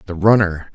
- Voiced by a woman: No, male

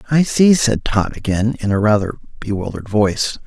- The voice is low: Yes, low, 115 Hz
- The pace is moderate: Yes, average, 175 wpm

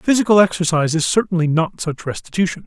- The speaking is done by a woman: No, male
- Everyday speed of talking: Yes, average, 160 wpm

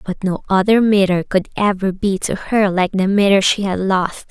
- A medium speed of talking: No, fast, 210 wpm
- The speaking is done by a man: No, female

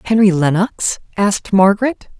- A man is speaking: No, female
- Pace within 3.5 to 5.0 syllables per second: Yes, 4.9 syllables/s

